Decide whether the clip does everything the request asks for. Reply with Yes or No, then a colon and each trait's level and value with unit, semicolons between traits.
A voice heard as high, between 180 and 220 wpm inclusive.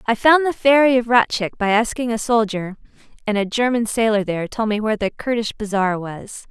Yes: high, 225 Hz; fast, 205 wpm